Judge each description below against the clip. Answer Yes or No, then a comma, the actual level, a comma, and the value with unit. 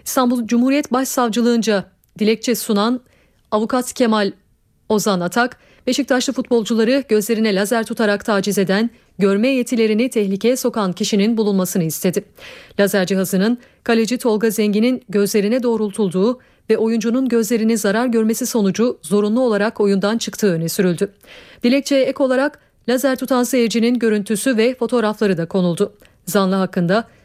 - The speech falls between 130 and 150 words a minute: No, average, 120 wpm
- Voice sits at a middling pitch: No, high, 225 Hz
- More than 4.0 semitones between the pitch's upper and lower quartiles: No, average, 3.2 semitones